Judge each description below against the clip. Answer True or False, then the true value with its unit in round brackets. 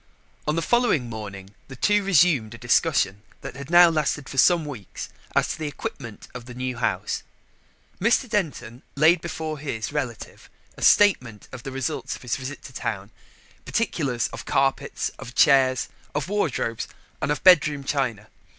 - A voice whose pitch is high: False (140 Hz)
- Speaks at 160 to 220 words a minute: True (165 wpm)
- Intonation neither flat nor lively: True (5.0 semitones)